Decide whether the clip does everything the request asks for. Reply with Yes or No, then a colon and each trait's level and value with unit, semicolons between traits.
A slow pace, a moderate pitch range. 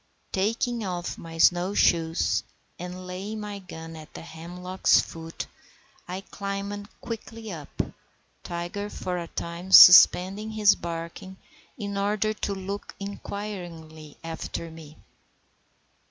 Yes: slow, 115 wpm; average, 3.3 semitones